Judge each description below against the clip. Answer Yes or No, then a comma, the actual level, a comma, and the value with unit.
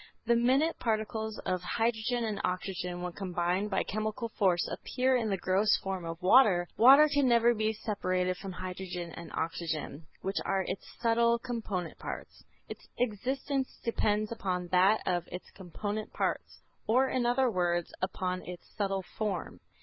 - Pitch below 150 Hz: No, high, 205 Hz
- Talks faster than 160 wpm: No, average, 155 wpm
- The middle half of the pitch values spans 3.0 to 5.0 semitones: Yes, average, 4.3 semitones